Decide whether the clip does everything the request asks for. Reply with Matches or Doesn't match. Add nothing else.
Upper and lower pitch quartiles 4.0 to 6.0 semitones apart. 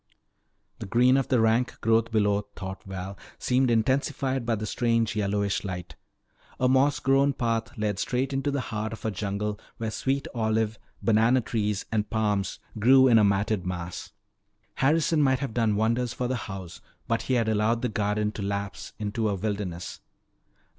Doesn't match